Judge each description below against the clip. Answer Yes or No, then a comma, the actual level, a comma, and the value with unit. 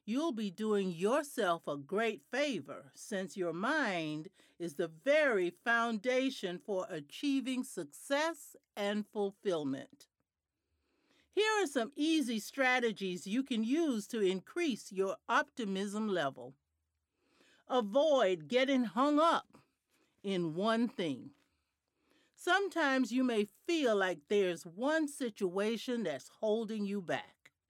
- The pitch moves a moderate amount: No, wide, 6.3 semitones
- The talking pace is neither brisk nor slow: No, slow, 110 wpm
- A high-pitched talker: Yes, high, 225 Hz